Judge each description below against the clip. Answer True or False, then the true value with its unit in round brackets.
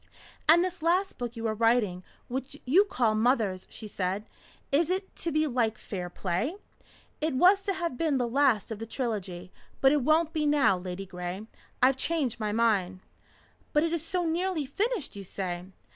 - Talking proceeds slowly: False (180 wpm)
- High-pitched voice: True (250 Hz)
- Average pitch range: False (7.8 semitones)